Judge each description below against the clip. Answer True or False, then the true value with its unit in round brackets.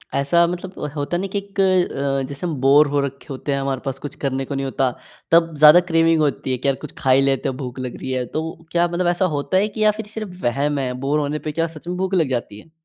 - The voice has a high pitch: False (145 Hz)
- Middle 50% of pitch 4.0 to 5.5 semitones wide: True (4.3 semitones)